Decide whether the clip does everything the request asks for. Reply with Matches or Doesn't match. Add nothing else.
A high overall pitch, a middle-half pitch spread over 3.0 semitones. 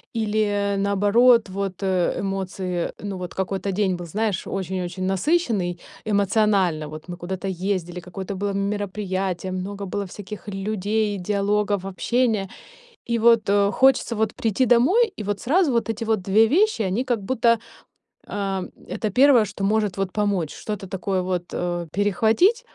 Doesn't match